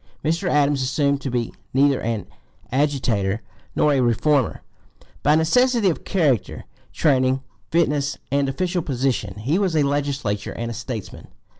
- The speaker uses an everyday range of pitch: Yes, average, 3.5 semitones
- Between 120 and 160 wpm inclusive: Yes, slow, 135 wpm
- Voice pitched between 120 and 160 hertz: Yes, medium, 140 Hz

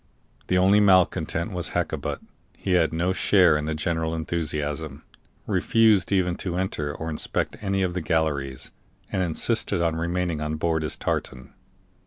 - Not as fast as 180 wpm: Yes, average, 155 wpm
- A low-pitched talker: Yes, very low, 85 Hz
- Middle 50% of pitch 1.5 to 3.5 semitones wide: Yes, average, 2.9 semitones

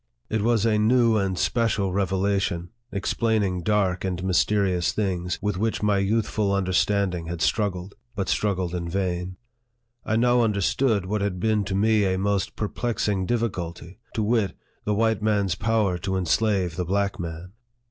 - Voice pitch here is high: No, low, 100 Hz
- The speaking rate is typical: Yes, average, 155 wpm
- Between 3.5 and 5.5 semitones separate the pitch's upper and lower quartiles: No, average, 2.7 semitones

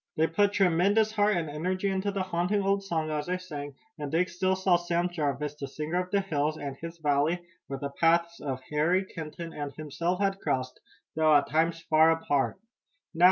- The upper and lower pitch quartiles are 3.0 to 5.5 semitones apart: Yes, average, 3.7 semitones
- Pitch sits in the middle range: Yes, medium, 165 Hz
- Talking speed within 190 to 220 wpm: Yes, average, 200 wpm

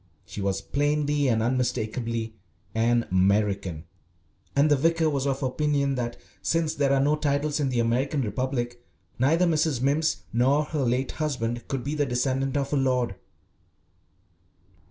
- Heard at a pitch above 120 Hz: Yes, low, 135 Hz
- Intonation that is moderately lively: Yes, average, 3.5 semitones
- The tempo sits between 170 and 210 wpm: No, average, 150 wpm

